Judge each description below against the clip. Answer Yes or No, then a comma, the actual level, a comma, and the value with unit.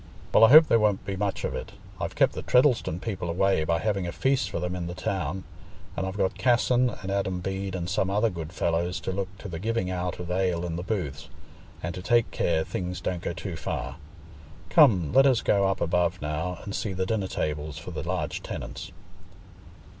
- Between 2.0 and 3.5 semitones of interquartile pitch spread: Yes, average, 2.9 semitones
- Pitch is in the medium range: No, very low, 95 Hz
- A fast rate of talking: Yes, fast, 215 wpm